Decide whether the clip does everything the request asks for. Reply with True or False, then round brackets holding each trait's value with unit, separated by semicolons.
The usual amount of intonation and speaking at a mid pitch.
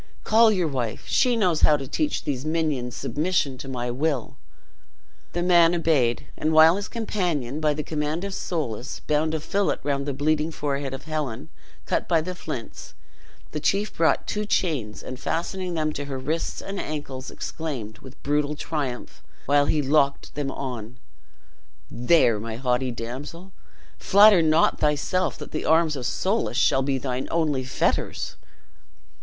True (4.0 semitones; 150 Hz)